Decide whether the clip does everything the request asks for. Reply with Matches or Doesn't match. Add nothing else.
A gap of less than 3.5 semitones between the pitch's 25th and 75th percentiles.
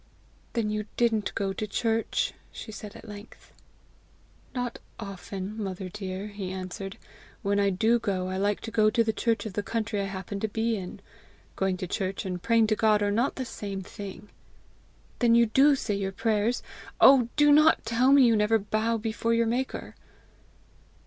Matches